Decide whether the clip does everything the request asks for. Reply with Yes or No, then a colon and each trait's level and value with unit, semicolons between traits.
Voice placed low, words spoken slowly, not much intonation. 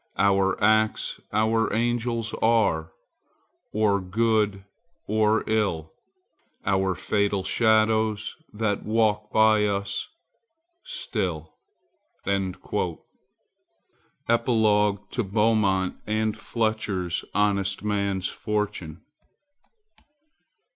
Yes: low, 105 Hz; slow, 70 wpm; narrow, 2.0 semitones